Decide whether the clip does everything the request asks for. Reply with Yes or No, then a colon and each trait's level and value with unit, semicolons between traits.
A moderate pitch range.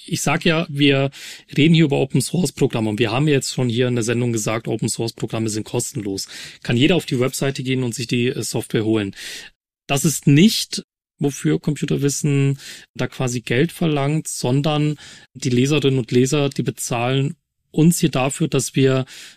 Yes: average, 3.6 semitones